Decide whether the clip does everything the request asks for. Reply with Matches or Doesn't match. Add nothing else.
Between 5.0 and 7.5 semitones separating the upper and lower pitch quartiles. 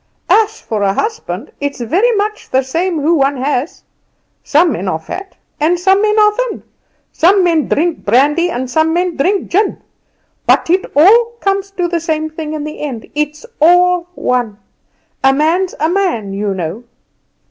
Matches